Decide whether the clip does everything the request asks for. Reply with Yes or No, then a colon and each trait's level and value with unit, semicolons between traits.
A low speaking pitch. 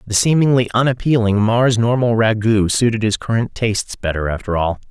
Yes: low, 110 Hz